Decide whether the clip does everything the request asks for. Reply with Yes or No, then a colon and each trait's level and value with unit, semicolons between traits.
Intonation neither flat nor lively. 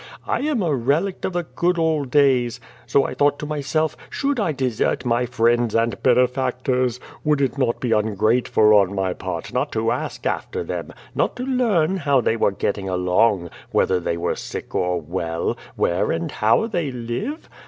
No: wide, 6.0 semitones